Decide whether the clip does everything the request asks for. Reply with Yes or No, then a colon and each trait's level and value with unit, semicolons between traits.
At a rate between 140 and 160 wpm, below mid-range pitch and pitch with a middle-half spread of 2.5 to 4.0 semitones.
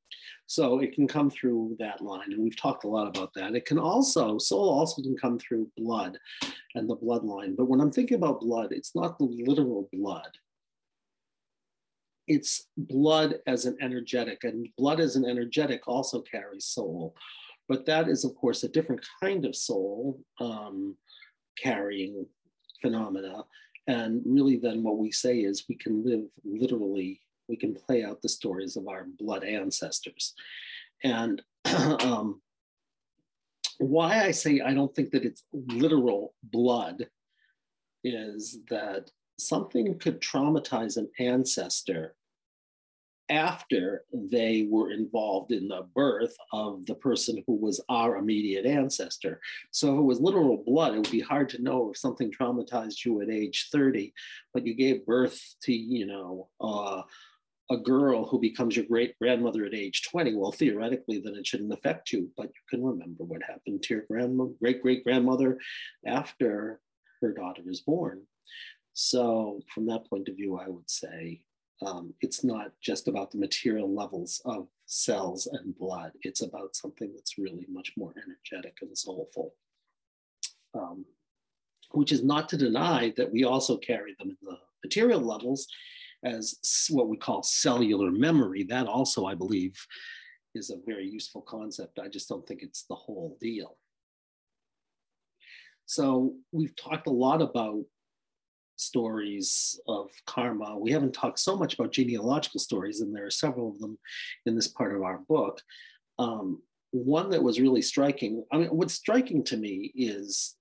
No: average, 155 wpm; low, 125 Hz; average, 4.5 semitones